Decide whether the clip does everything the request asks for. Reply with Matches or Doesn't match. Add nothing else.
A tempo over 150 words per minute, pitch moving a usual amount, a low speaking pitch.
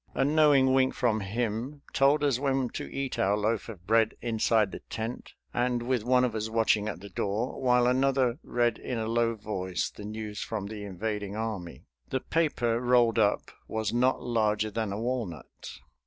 Matches